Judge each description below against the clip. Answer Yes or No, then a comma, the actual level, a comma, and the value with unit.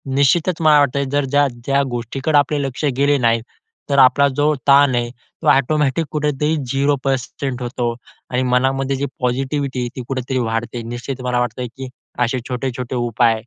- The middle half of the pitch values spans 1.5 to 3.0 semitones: Yes, narrow, 2.5 semitones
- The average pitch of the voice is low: Yes, low, 130 Hz